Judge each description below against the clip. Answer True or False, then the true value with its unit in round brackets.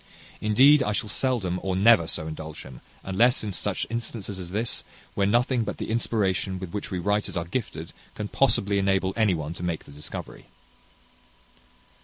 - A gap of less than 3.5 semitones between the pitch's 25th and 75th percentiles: False (4.1 semitones)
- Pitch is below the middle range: True (100 Hz)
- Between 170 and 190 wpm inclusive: True (175 wpm)